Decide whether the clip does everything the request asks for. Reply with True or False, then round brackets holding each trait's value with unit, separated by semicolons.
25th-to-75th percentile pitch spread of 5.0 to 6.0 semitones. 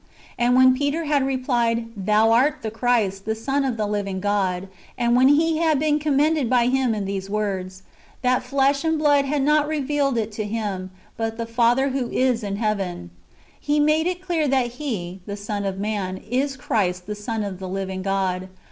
True (5.5 semitones)